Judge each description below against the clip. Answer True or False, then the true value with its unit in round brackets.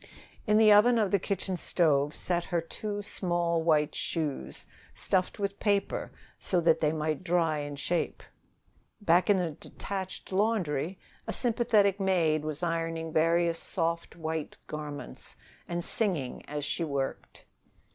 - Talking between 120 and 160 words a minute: True (140 wpm)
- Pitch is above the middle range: False (170 Hz)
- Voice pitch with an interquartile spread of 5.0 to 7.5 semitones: False (3.9 semitones)